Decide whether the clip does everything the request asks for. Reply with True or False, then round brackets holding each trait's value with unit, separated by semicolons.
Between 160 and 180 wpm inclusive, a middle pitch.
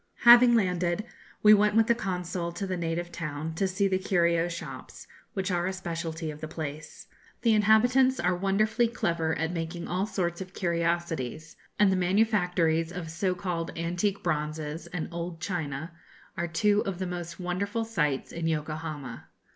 True (165 wpm; 175 Hz)